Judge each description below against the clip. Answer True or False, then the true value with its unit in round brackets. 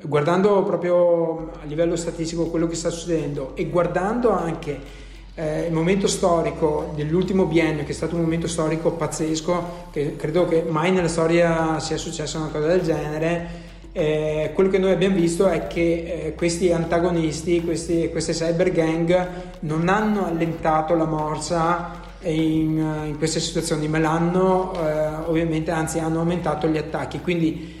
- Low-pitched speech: False (165 Hz)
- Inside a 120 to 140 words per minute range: False (155 wpm)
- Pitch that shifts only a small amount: True (1.6 semitones)